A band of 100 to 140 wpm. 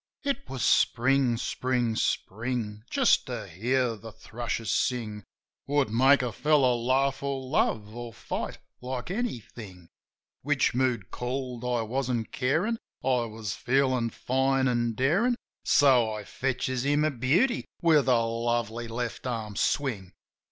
Yes: slow, 135 wpm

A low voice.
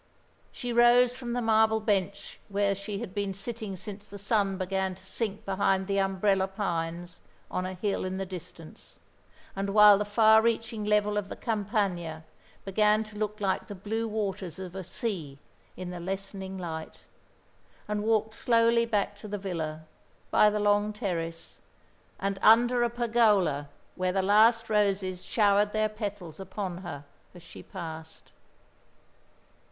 No: high, 200 Hz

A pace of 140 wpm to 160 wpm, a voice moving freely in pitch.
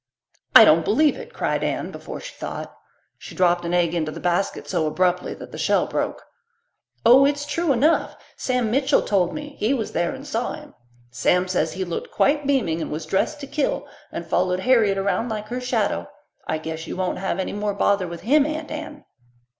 No: average, 200 wpm; wide, 7.9 semitones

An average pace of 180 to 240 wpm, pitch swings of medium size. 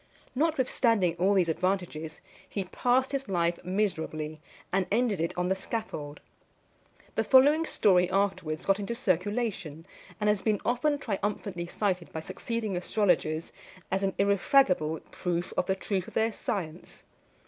No: average, 140 wpm; average, 4.2 semitones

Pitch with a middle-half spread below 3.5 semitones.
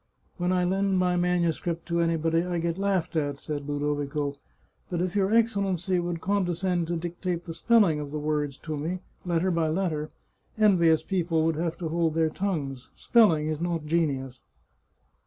Yes: average, 2.8 semitones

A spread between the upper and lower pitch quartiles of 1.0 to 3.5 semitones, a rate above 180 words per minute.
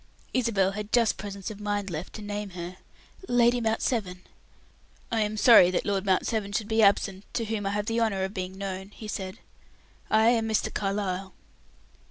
Yes: narrow, 2.4 semitones; average, 190 wpm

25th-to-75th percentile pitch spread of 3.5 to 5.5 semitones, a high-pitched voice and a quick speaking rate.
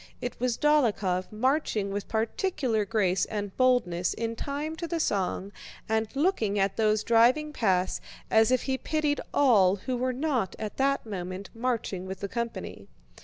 No: average, 4.8 semitones; high, 225 Hz; average, 160 wpm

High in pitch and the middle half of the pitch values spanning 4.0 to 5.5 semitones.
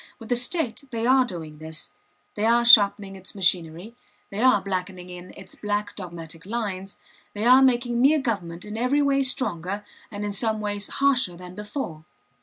Yes: high, 205 Hz; average, 4.8 semitones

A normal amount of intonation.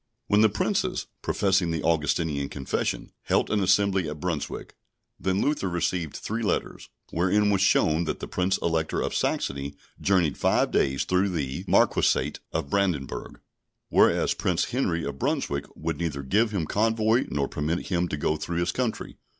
Yes: average, 4.6 semitones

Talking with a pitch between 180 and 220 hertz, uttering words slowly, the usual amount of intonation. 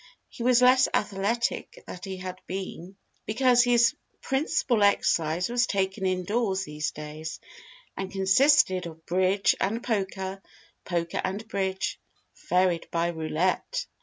Yes: high, 190 Hz; slow, 125 wpm; average, 4.4 semitones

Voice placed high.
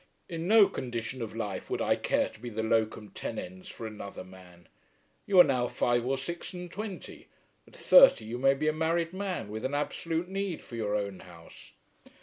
No: low, 125 Hz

